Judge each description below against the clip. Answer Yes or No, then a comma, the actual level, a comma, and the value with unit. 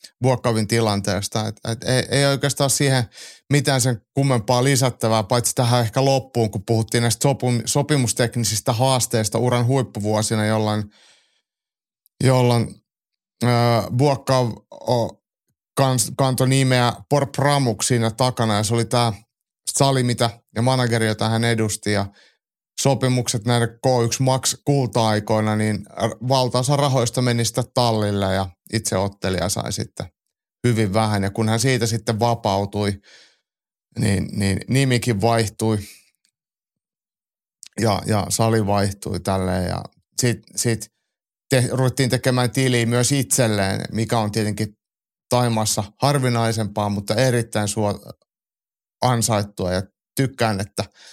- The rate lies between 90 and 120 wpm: Yes, average, 115 wpm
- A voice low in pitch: Yes, low, 115 Hz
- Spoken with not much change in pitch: No, average, 3.0 semitones